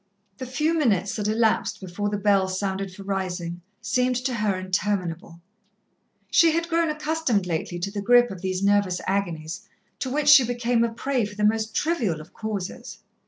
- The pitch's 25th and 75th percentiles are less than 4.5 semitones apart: No, average, 4.8 semitones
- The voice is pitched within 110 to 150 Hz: No, high, 205 Hz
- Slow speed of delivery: No, average, 175 wpm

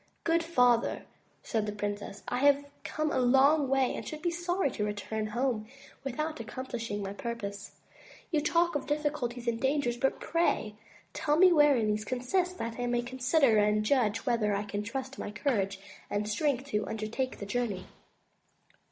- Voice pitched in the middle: No, high, 245 Hz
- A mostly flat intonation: No, average, 5.3 semitones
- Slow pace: No, average, 170 wpm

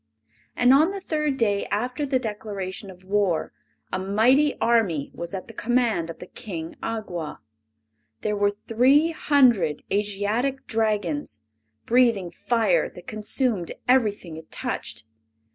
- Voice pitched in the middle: No, high, 215 Hz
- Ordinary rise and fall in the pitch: Yes, average, 5.0 semitones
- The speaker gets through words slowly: Yes, slow, 130 wpm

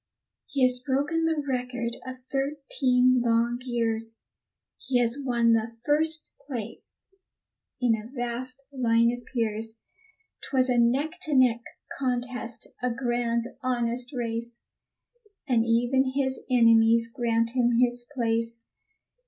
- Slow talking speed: Yes, slow, 120 wpm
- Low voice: No, high, 245 Hz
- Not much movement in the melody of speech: Yes, narrow, 2.0 semitones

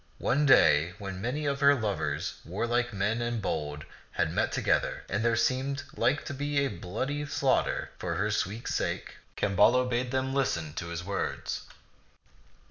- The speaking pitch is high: No, low, 115 Hz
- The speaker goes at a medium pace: Yes, average, 160 wpm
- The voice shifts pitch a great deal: Yes, wide, 5.7 semitones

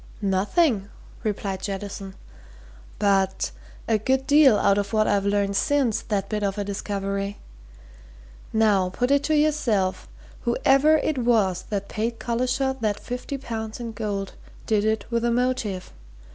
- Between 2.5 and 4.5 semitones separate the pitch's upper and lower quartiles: Yes, average, 3.9 semitones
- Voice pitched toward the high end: Yes, high, 215 Hz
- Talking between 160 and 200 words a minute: No, average, 145 wpm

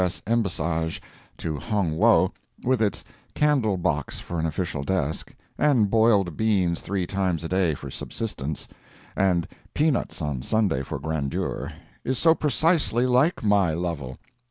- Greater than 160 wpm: No, average, 140 wpm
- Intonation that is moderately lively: No, wide, 5.9 semitones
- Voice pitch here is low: Yes, very low, 95 Hz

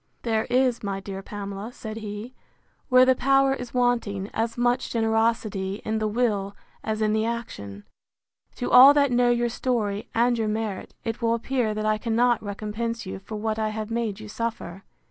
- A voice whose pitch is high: Yes, high, 225 Hz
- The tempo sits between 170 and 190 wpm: Yes, average, 185 wpm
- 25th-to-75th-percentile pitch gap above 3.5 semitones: No, narrow, 2.5 semitones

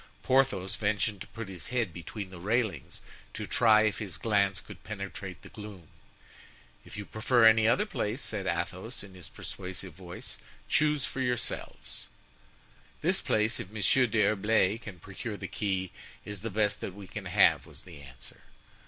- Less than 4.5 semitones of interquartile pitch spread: Yes, average, 3.2 semitones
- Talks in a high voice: No, low, 105 Hz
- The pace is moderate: Yes, average, 165 wpm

